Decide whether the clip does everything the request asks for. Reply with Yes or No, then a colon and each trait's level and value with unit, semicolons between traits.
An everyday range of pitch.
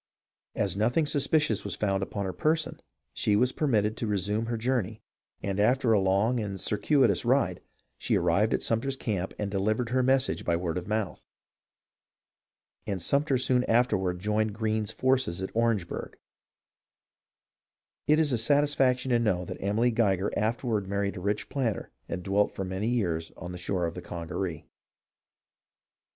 Yes: average, 4.5 semitones